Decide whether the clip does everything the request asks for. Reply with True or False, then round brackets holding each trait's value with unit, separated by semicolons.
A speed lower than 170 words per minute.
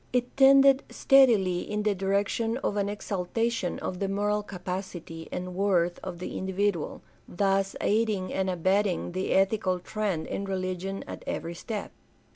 True (150 wpm)